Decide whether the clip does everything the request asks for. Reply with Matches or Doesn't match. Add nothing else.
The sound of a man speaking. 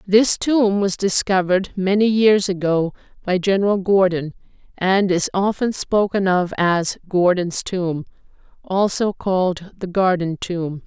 Doesn't match